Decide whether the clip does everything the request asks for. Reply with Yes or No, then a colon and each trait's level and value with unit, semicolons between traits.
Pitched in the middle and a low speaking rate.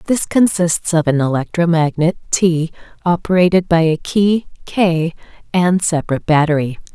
Yes: medium, 170 Hz; slow, 120 wpm